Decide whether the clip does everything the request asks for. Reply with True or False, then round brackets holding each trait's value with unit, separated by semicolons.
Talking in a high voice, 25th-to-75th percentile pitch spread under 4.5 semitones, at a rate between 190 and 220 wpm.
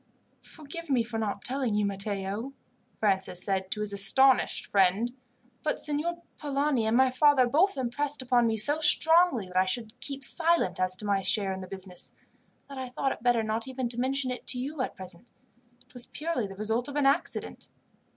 False (245 Hz; 5.4 semitones; 195 wpm)